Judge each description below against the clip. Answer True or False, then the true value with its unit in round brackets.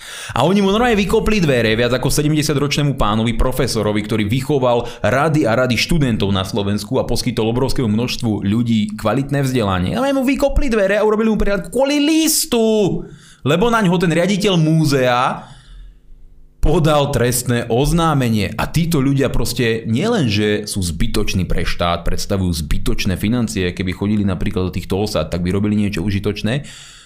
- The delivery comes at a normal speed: True (150 wpm)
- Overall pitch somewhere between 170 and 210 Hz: False (120 Hz)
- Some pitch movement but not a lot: False (7.1 semitones)